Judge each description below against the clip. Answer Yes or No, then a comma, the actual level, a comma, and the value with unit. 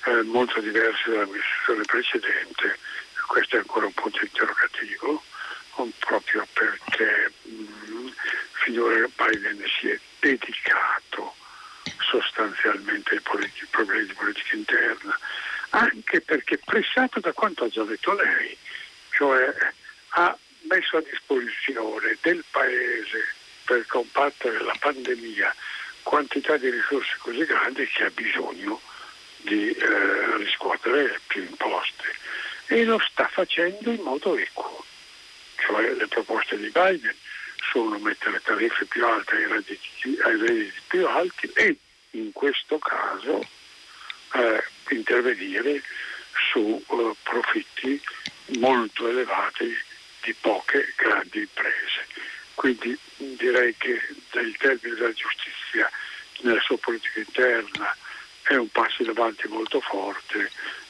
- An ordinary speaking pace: No, slow, 110 wpm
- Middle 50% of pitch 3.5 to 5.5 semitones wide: Yes, average, 5.1 semitones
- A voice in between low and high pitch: No, very high, 365 Hz